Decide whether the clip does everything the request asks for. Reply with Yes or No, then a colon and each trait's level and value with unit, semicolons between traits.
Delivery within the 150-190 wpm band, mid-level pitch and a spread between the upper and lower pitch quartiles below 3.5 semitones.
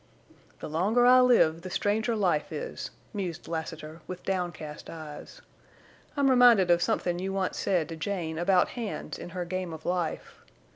No: average, 160 wpm; medium, 180 Hz; average, 3.9 semitones